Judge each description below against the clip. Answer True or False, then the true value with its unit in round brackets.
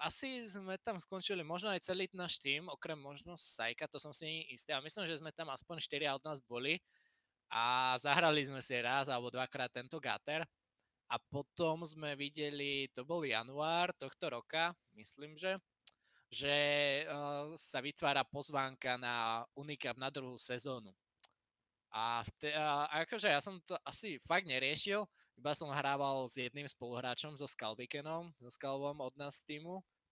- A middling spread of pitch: True (3.9 semitones)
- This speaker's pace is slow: False (155 wpm)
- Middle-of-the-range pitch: True (145 Hz)